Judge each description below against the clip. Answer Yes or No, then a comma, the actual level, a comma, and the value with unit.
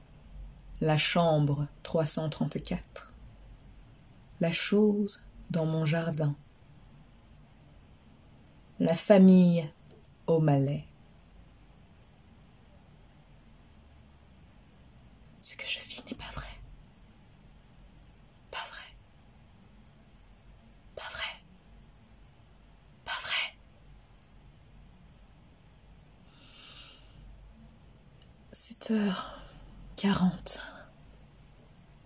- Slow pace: Yes, slow, 50 wpm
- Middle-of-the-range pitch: Yes, medium, 155 Hz